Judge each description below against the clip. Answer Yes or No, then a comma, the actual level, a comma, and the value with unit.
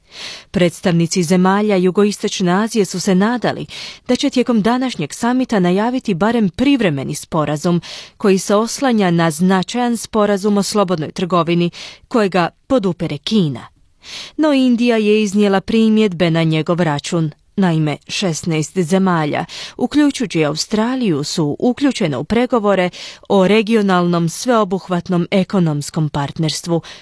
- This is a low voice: No, high, 190 Hz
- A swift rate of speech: No, slow, 110 wpm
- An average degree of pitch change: Yes, average, 4.3 semitones